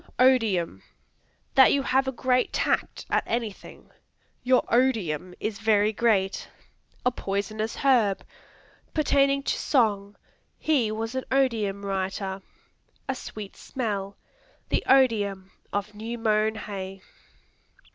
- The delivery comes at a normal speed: No, slow, 115 wpm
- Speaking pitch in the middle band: No, high, 220 Hz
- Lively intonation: No, average, 4.2 semitones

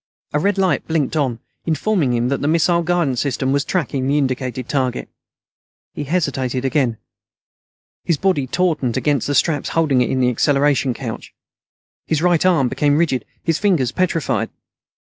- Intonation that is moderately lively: Yes, average, 4.2 semitones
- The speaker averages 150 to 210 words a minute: Yes, average, 160 wpm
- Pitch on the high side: No, medium, 145 Hz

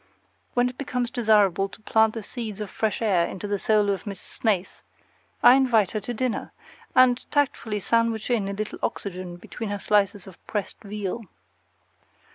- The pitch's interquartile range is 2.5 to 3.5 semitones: Yes, average, 2.8 semitones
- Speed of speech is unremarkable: Yes, average, 170 wpm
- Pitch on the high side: Yes, high, 215 Hz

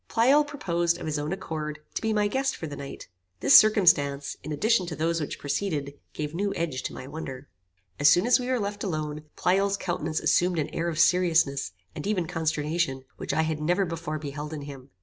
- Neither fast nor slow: No, fast, 210 wpm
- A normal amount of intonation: Yes, average, 4.5 semitones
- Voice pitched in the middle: Yes, medium, 165 Hz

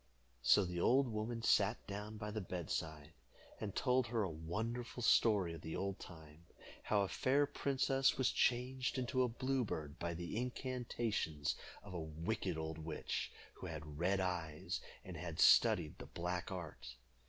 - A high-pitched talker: No, low, 100 Hz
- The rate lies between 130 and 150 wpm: No, average, 165 wpm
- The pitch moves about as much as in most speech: No, wide, 6.7 semitones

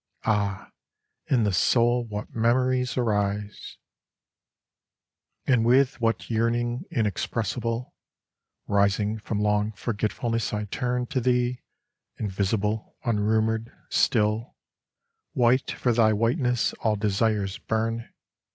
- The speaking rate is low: Yes, slow, 95 wpm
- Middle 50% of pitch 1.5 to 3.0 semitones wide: Yes, narrow, 2.5 semitones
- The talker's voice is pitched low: Yes, low, 115 Hz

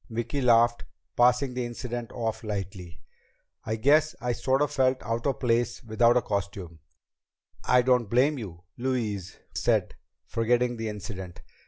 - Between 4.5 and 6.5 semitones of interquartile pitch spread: No, average, 2.7 semitones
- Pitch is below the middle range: Yes, low, 120 Hz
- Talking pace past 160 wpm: No, average, 145 wpm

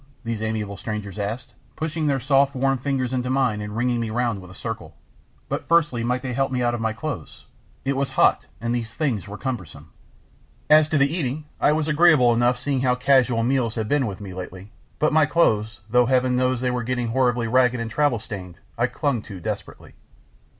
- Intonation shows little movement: No, average, 3.4 semitones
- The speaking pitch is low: Yes, low, 125 Hz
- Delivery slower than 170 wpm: No, fast, 205 wpm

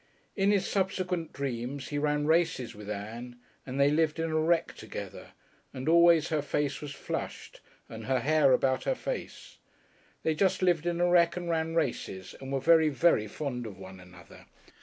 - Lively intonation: No, average, 4.8 semitones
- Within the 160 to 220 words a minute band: Yes, average, 180 wpm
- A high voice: No, medium, 150 Hz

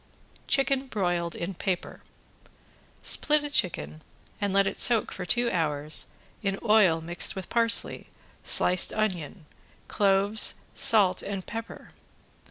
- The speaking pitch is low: No, high, 195 Hz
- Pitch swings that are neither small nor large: Yes, average, 4.1 semitones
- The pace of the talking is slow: Yes, slow, 120 wpm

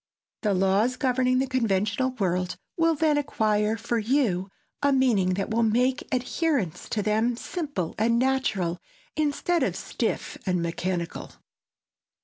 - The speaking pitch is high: Yes, high, 230 Hz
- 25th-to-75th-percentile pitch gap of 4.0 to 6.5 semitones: Yes, average, 5.3 semitones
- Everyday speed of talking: No, slow, 130 wpm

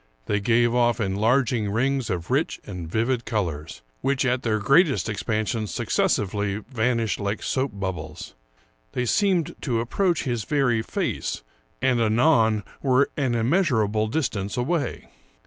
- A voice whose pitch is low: Yes, low, 115 Hz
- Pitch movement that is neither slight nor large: Yes, average, 3.9 semitones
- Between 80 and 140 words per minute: Yes, slow, 135 wpm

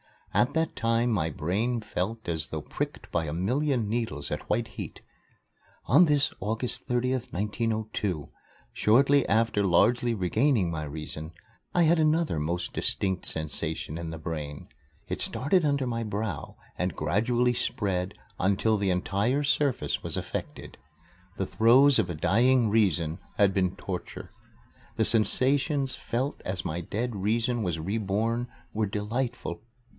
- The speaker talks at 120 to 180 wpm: Yes, average, 140 wpm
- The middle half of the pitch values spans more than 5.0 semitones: Yes, wide, 5.4 semitones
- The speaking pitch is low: Yes, low, 110 Hz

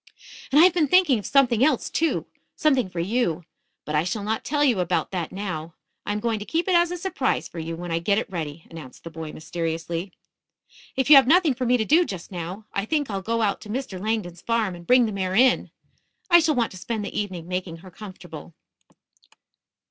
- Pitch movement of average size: No, wide, 6.9 semitones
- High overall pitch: Yes, high, 205 Hz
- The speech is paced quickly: Yes, fast, 225 wpm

